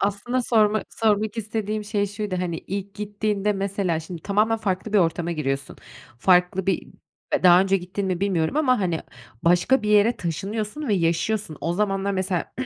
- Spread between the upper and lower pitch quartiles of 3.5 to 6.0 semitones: No, average, 3.0 semitones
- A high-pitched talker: Yes, high, 200 Hz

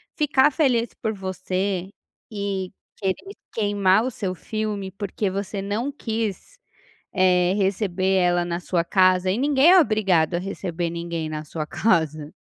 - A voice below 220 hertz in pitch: Yes, high, 190 Hz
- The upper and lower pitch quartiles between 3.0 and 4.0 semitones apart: Yes, average, 3.3 semitones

